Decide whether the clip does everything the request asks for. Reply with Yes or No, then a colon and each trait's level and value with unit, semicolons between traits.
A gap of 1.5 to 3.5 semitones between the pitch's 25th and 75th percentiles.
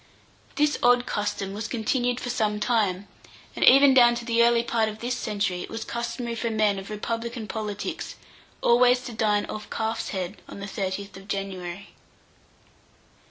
Yes: average, 2.8 semitones